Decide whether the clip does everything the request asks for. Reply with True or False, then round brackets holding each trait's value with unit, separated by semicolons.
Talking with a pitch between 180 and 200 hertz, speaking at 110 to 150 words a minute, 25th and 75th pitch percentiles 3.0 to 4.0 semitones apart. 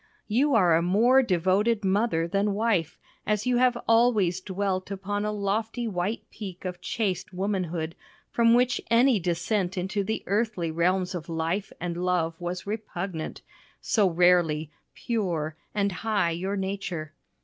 True (190 Hz; 145 wpm; 3.4 semitones)